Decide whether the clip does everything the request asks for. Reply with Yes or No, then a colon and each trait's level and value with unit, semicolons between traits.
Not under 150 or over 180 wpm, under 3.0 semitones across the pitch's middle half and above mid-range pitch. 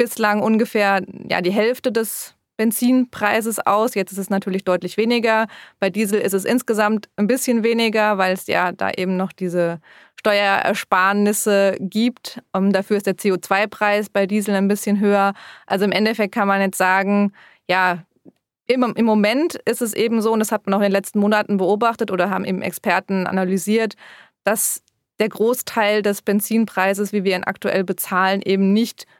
Yes: average, 170 wpm; narrow, 2.4 semitones; high, 205 Hz